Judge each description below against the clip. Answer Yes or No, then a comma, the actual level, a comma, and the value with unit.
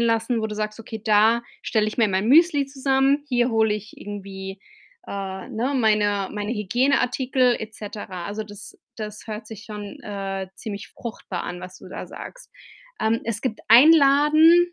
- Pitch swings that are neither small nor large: Yes, average, 3.6 semitones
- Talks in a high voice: Yes, high, 220 Hz